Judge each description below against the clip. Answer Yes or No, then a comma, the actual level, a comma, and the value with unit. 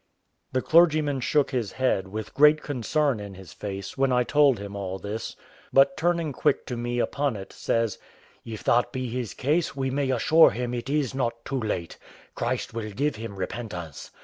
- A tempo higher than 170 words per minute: Yes, average, 185 wpm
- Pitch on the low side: Yes, low, 125 Hz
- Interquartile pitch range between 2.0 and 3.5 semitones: No, average, 4.8 semitones